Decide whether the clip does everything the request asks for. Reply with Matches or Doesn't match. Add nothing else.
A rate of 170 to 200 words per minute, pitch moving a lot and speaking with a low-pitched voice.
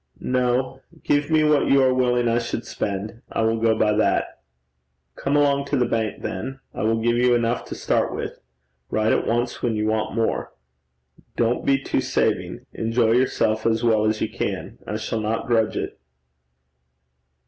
Doesn't match